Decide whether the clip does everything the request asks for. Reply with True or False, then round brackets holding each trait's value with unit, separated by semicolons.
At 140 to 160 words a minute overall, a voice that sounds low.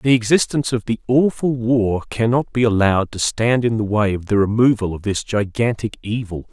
False (195 wpm; 115 Hz)